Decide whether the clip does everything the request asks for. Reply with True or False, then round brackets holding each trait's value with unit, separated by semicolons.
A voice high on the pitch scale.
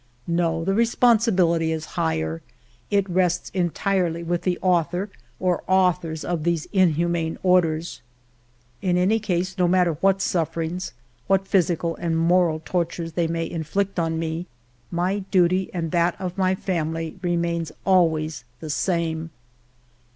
False (175 Hz)